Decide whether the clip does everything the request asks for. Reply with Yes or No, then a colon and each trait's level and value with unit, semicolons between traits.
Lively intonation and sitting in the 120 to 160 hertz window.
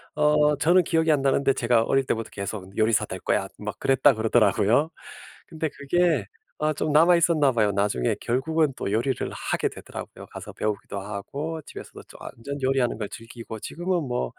Yes: wide, 5.7 semitones; low, 135 Hz